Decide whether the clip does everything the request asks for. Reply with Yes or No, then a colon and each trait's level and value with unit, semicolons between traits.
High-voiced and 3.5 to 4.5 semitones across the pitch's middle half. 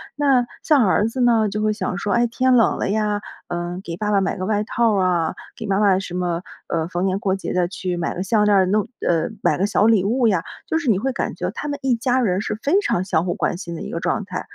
Yes: high, 205 Hz; average, 4.0 semitones